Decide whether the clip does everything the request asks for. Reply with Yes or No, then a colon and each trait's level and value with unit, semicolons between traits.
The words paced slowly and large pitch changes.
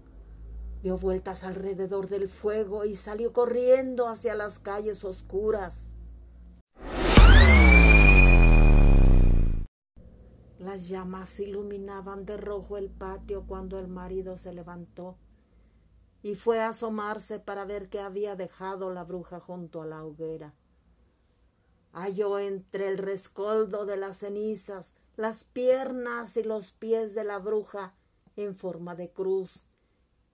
No: slow, 115 wpm; average, 3.0 semitones